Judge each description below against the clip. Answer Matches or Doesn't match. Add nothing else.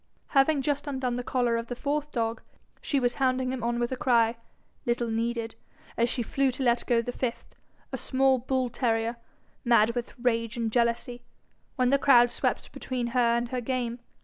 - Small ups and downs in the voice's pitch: Matches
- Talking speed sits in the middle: Matches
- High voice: Matches